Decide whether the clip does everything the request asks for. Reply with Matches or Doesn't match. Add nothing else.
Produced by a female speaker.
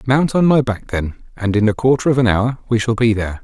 Doesn't match